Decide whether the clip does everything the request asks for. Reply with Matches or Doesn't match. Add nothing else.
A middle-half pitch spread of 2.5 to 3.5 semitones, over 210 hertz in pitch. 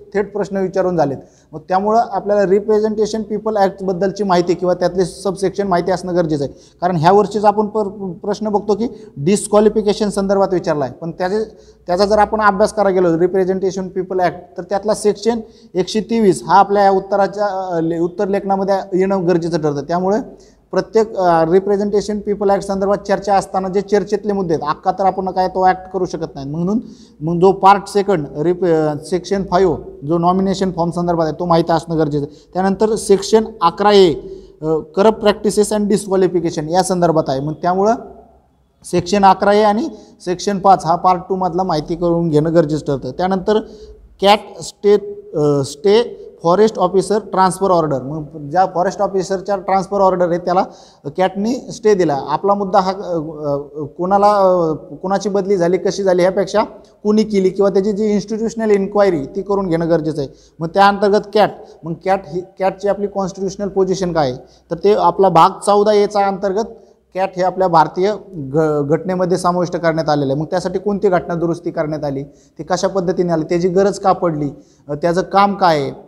Doesn't match